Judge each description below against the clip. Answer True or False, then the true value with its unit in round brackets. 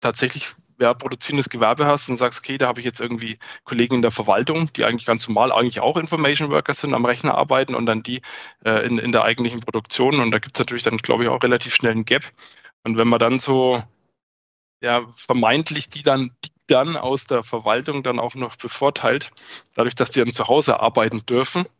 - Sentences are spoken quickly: True (215 wpm)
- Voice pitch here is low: True (125 Hz)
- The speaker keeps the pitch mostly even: False (3.1 semitones)